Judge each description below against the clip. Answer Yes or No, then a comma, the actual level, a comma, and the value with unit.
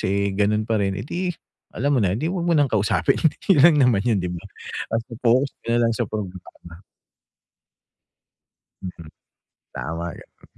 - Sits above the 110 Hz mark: No, low, 105 Hz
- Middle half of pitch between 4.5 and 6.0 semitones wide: Yes, average, 5.1 semitones